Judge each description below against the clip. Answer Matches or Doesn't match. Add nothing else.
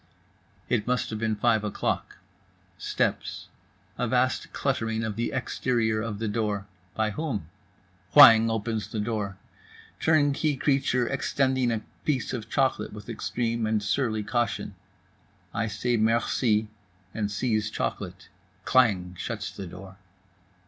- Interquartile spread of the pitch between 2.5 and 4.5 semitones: Matches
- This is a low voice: Matches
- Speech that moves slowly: Matches